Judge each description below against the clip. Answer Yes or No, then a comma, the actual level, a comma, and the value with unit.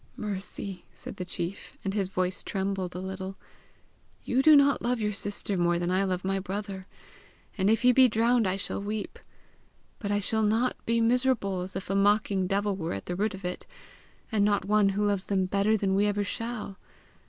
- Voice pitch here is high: Yes, high, 200 Hz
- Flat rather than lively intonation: Yes, narrow, 2.2 semitones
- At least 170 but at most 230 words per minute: Yes, average, 200 wpm